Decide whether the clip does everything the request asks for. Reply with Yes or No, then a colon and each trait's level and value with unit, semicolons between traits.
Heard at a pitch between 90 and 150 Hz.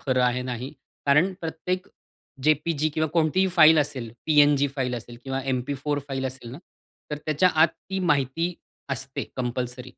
Yes: medium, 140 Hz